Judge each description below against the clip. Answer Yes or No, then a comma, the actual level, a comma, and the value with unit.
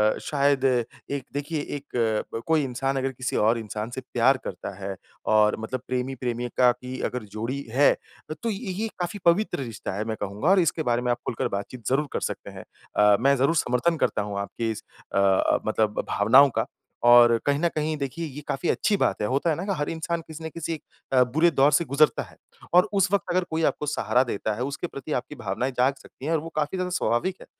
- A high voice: No, low, 135 Hz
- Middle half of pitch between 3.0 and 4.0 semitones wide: No, average, 5.2 semitones